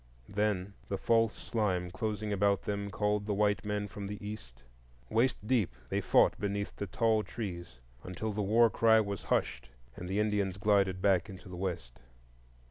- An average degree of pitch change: No, narrow, 2.3 semitones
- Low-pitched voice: Yes, low, 100 Hz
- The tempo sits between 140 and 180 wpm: Yes, average, 170 wpm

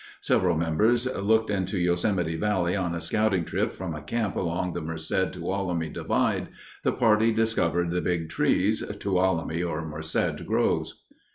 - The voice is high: No, very low, 90 Hz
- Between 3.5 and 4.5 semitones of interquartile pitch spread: Yes, average, 3.9 semitones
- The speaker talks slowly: No, average, 150 wpm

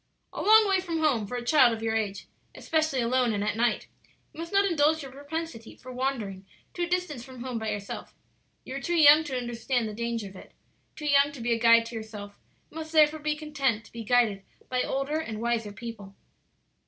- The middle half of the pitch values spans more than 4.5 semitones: Yes, average, 5.2 semitones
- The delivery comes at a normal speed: No, fast, 220 wpm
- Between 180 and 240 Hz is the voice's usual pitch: No, very high, 250 Hz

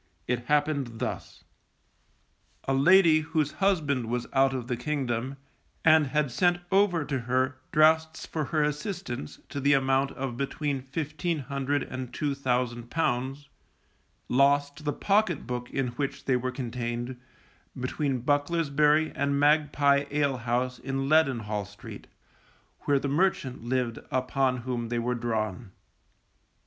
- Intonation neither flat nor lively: Yes, average, 3.2 semitones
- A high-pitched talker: No, low, 135 Hz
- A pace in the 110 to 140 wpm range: Yes, slow, 135 wpm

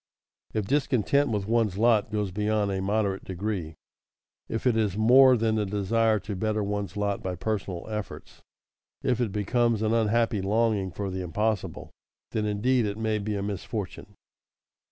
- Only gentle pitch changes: Yes, narrow, 2.1 semitones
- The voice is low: Yes, low, 105 Hz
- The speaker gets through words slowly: No, average, 160 wpm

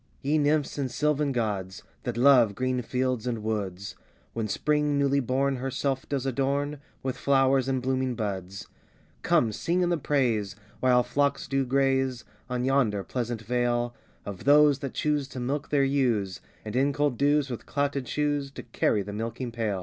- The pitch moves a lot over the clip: No, average, 3.2 semitones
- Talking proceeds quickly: No, average, 170 wpm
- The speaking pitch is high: No, low, 130 Hz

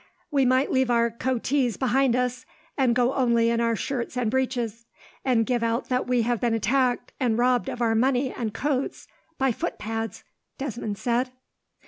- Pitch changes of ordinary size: No, narrow, 1.9 semitones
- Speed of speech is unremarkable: Yes, average, 170 wpm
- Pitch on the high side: Yes, high, 245 Hz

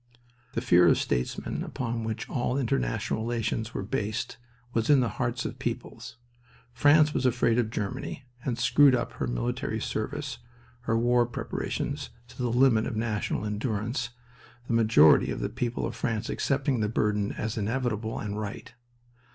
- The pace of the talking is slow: No, average, 160 wpm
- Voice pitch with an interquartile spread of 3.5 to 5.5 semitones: No, narrow, 2.5 semitones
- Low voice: Yes, low, 115 Hz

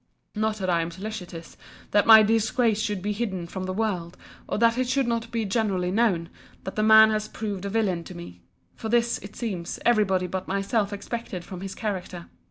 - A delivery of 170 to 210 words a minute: Yes, fast, 205 wpm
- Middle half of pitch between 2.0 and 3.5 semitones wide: Yes, average, 3.2 semitones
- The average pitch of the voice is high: Yes, high, 205 Hz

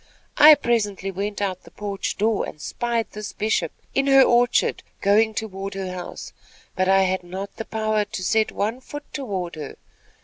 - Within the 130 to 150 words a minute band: No, average, 180 wpm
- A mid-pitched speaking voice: No, high, 205 Hz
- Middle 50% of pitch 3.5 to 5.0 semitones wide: No, average, 2.8 semitones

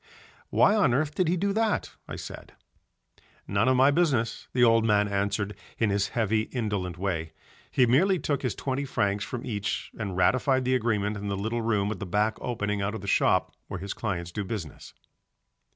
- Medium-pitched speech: No, low, 110 Hz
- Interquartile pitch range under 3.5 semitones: No, average, 4.3 semitones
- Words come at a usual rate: Yes, average, 195 wpm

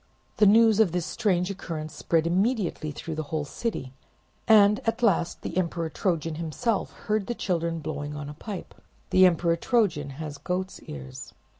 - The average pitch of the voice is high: No, medium, 170 Hz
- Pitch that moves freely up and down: No, average, 4.7 semitones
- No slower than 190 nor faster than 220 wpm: No, average, 165 wpm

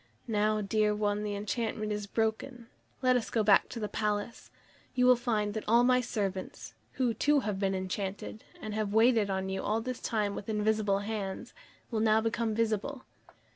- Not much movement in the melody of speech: Yes, narrow, 1.9 semitones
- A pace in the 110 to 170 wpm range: No, average, 185 wpm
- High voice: Yes, high, 215 Hz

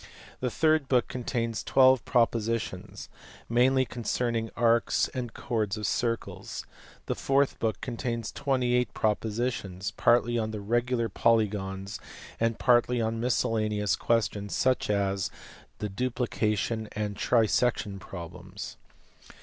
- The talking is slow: Yes, slow, 110 wpm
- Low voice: Yes, low, 115 Hz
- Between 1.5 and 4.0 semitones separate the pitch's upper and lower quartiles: Yes, average, 2.8 semitones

